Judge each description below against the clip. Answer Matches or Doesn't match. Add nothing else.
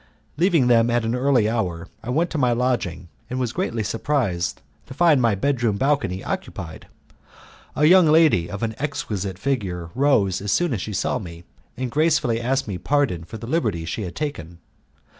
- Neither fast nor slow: Matches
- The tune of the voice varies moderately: Doesn't match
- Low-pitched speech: Matches